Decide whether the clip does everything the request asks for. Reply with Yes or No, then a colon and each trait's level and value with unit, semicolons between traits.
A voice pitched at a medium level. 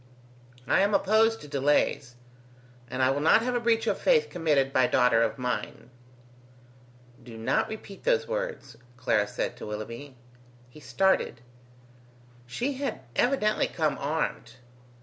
Yes: medium, 145 Hz